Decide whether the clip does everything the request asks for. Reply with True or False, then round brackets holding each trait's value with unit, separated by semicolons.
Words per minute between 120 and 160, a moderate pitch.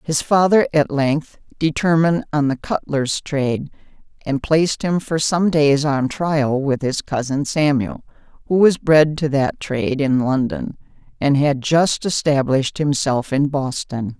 True (150 wpm; 145 Hz)